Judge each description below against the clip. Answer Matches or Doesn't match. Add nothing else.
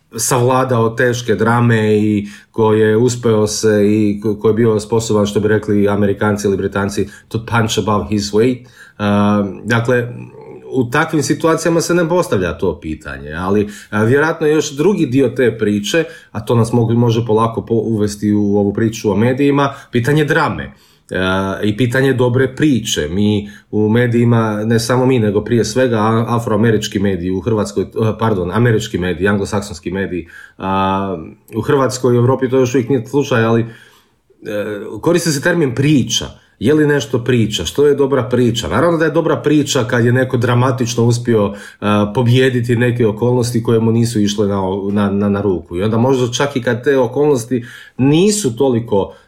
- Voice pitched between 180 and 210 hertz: Doesn't match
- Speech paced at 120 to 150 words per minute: Doesn't match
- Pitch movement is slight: Doesn't match